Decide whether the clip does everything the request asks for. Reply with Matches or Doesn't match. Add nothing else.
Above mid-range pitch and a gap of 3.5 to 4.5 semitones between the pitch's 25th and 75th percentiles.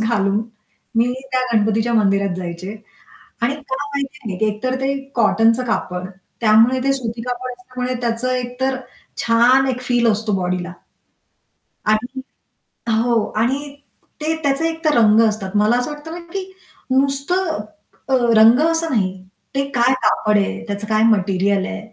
Matches